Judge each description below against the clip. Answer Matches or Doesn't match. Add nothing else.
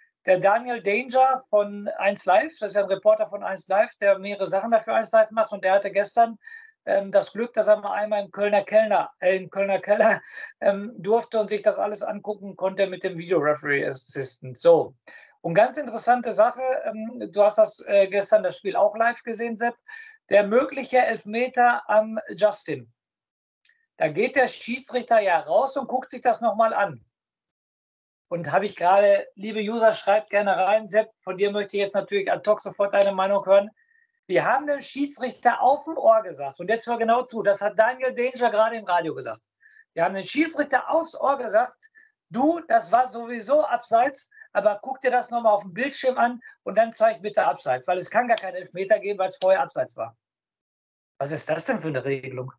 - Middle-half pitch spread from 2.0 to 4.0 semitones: Doesn't match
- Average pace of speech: Doesn't match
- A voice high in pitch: Matches